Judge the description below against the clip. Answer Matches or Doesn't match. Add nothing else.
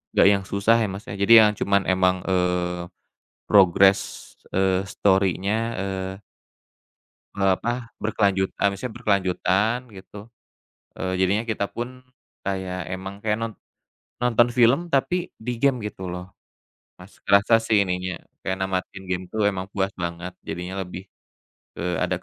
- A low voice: Matches